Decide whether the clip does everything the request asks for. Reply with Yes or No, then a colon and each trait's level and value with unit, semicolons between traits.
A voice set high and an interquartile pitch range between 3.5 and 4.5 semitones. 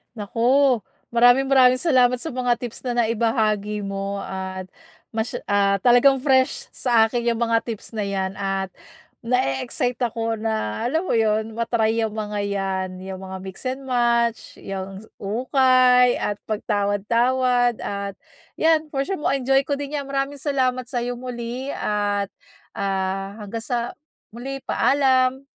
Yes: high, 235 Hz; average, 3.9 semitones